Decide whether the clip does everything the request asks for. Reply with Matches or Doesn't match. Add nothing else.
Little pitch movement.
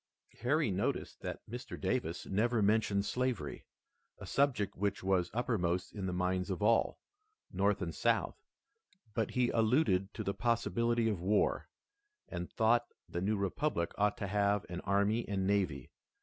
Doesn't match